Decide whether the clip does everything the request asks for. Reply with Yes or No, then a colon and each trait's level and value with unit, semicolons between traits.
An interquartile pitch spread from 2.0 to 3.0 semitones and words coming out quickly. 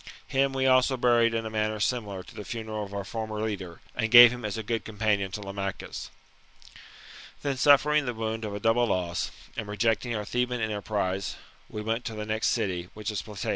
Yes: narrow, 2.6 semitones; fast, 210 wpm